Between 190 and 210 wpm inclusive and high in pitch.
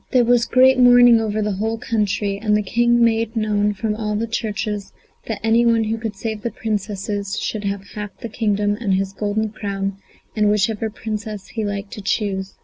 Yes: average, 200 wpm; high, 215 Hz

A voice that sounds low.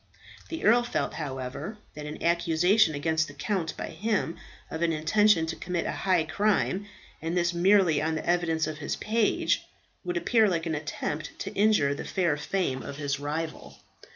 No: medium, 165 Hz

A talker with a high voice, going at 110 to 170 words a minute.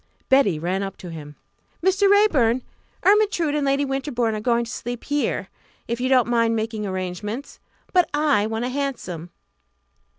Yes: high, 240 Hz; average, 160 wpm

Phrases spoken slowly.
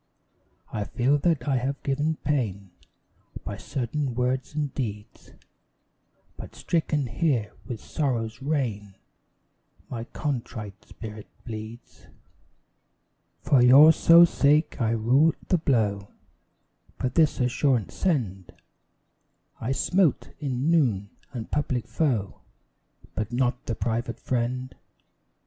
Yes: slow, 110 wpm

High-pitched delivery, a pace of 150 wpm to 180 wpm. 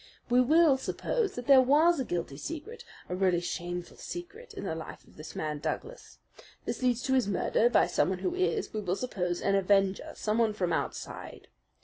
No: high, 240 Hz; average, 190 wpm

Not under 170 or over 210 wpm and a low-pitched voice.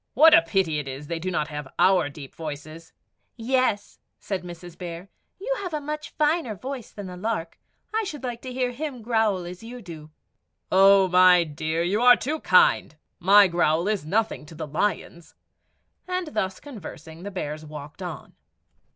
No: average, 175 wpm; medium, 185 Hz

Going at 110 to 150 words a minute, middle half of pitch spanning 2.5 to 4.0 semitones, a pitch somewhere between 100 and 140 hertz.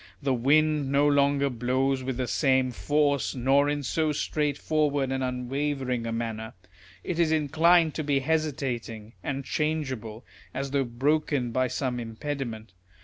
Yes: average, 145 wpm; average, 2.9 semitones; low, 135 Hz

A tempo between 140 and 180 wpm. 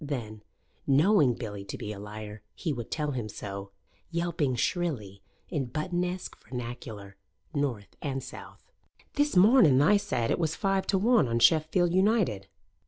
Yes: average, 150 wpm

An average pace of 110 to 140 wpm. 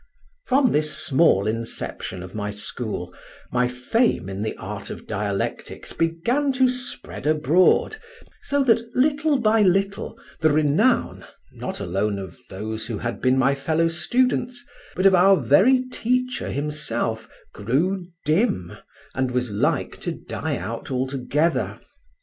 Yes: slow, 135 wpm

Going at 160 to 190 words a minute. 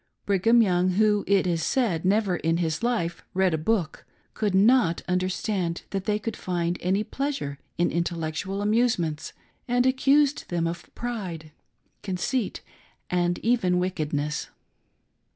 No: slow, 135 wpm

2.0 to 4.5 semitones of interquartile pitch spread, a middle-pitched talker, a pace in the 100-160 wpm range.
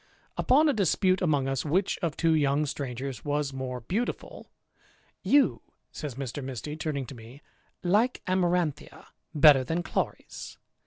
No: average, 4.9 semitones; medium, 150 Hz; average, 150 wpm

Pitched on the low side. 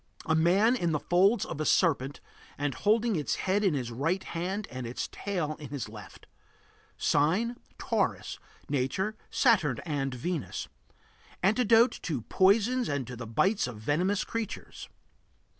No: medium, 170 Hz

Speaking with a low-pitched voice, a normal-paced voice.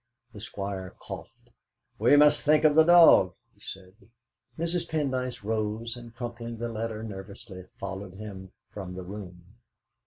Yes: low, 110 Hz; average, 145 wpm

